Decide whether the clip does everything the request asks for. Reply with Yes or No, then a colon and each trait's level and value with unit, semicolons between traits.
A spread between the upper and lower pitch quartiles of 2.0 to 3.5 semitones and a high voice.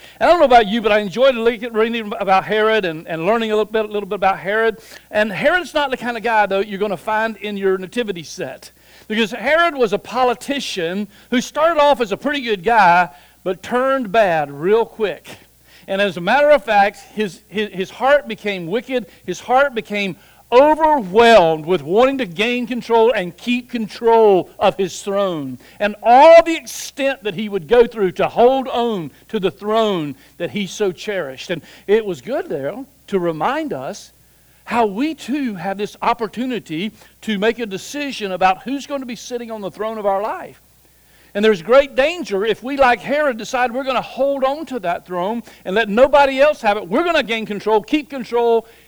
No: average, 4.2 semitones; high, 220 Hz